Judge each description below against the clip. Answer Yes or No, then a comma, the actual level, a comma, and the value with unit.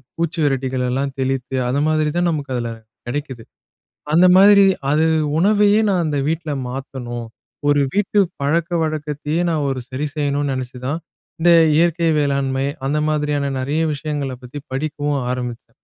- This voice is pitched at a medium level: Yes, medium, 145 Hz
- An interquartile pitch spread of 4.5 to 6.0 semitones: No, average, 3.3 semitones